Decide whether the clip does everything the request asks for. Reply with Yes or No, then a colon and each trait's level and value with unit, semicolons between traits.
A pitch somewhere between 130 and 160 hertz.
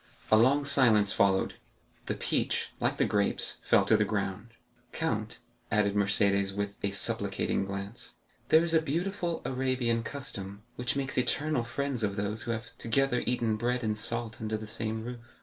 No: low, 115 Hz